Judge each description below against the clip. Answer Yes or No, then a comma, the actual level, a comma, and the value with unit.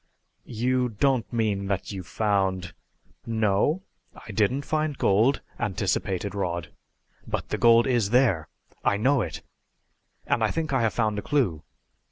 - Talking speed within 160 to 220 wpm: No, average, 150 wpm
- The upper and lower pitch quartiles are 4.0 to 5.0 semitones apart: Yes, average, 4.6 semitones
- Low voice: Yes, low, 110 Hz